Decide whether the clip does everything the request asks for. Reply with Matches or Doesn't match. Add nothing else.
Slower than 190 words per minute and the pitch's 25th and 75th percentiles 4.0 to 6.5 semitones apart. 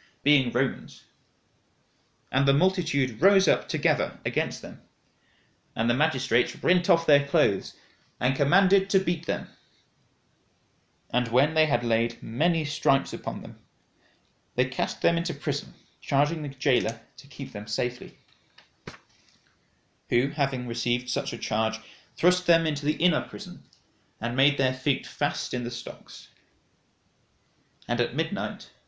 Matches